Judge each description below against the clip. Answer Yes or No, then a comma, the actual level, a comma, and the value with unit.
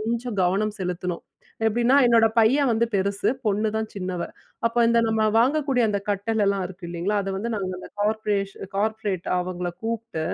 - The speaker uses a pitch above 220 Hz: No, high, 210 Hz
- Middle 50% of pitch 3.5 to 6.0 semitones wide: No, average, 3.1 semitones